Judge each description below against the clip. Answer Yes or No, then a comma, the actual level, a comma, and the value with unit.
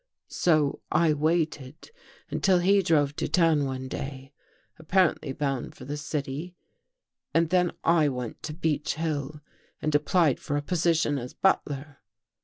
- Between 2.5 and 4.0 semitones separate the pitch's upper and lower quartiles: Yes, average, 2.9 semitones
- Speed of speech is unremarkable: Yes, average, 145 wpm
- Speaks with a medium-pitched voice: Yes, medium, 150 Hz